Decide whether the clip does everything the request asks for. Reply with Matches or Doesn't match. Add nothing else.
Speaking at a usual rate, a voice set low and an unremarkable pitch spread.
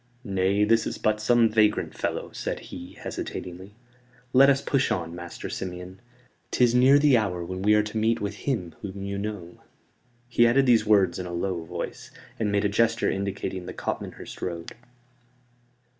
Matches